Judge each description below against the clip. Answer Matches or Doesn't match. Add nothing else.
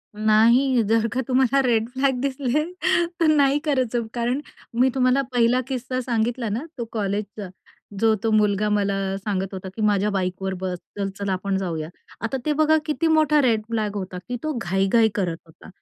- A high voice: Matches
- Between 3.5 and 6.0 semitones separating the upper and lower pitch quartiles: Matches